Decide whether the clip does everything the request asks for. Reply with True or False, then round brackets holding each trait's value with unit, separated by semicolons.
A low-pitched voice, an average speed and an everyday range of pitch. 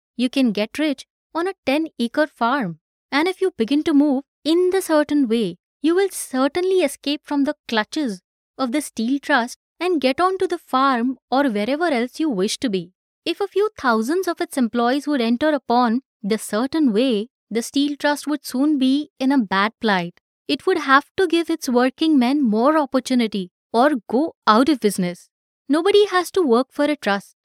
False (275 Hz; 190 wpm; 4.6 semitones)